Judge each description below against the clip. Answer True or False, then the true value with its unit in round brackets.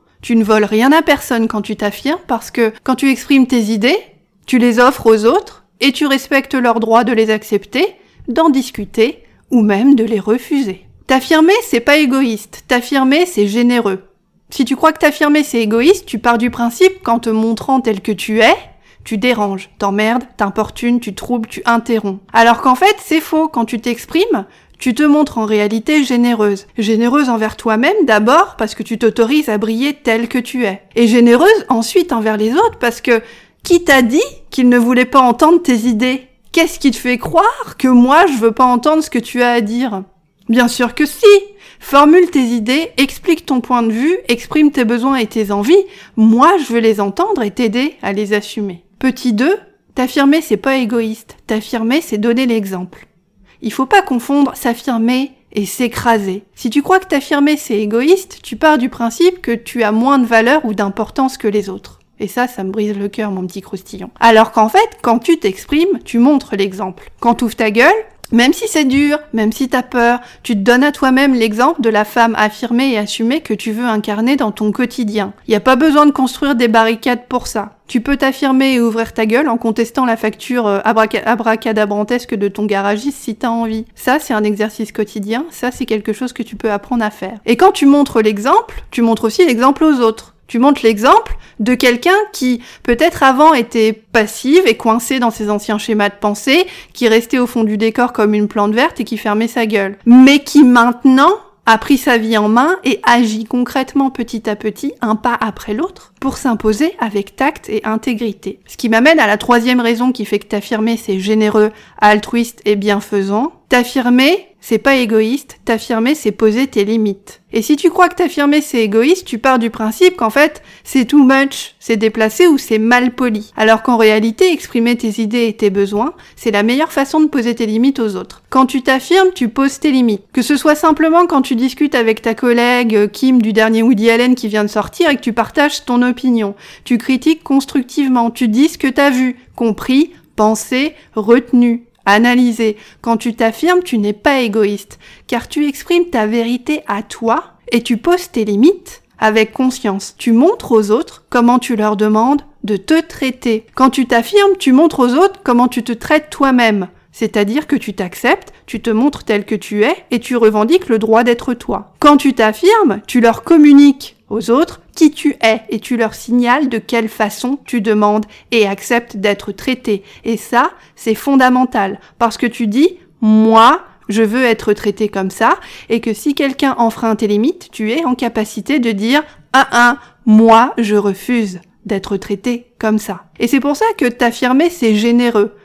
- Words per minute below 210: True (195 wpm)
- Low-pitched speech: False (240 Hz)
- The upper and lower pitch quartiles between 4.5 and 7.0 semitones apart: False (4.0 semitones)